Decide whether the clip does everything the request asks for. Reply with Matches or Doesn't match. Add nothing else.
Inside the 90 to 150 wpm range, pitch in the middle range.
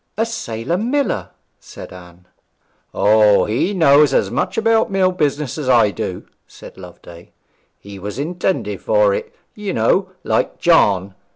Matches